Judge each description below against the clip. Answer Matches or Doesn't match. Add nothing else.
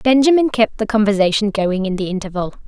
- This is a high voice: Matches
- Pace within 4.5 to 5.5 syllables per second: Doesn't match